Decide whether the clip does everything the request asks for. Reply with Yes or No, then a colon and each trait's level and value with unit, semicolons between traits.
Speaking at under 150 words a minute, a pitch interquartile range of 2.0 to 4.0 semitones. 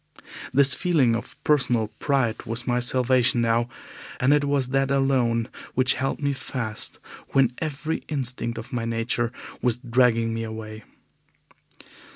Yes: average, 140 wpm; average, 2.9 semitones